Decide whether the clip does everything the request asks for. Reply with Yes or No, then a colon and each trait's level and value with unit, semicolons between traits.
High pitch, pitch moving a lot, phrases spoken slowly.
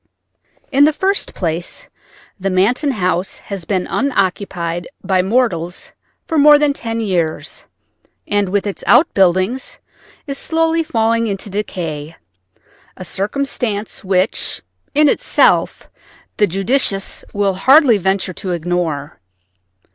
Yes: high, 200 Hz; wide, 5.8 semitones; slow, 110 wpm